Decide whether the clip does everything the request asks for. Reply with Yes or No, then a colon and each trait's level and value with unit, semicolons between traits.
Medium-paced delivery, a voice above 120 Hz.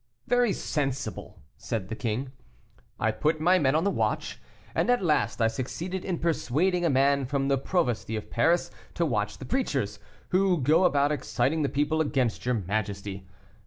Yes: average, 165 wpm; medium, 140 Hz